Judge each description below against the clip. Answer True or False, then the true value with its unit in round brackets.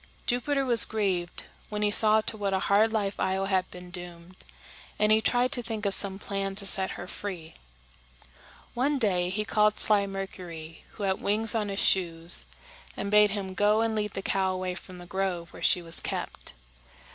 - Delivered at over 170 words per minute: True (190 wpm)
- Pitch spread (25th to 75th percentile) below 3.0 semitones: True (2.5 semitones)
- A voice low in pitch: False (195 Hz)